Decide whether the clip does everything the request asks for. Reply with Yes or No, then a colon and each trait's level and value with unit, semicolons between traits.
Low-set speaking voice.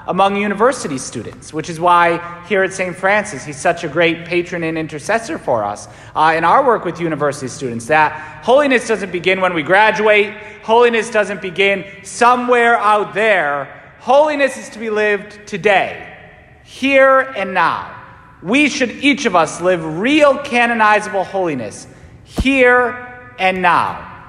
No: high, 195 Hz